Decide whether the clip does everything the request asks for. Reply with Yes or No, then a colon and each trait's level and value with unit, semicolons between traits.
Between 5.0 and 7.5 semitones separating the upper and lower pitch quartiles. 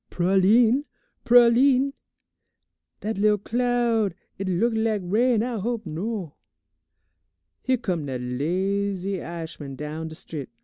Yes: wide, 5.5 semitones